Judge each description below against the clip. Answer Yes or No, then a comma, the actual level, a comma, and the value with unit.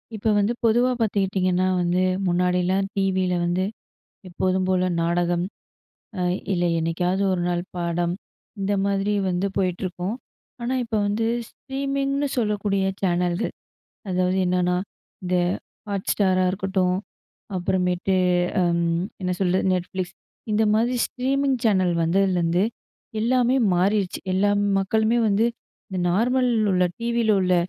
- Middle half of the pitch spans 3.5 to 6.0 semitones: No, average, 3.1 semitones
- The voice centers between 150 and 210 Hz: Yes, high, 190 Hz